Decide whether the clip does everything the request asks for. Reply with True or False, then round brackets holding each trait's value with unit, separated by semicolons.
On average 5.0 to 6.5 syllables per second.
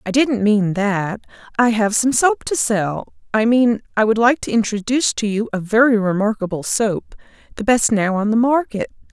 False (4.8 syllables/s)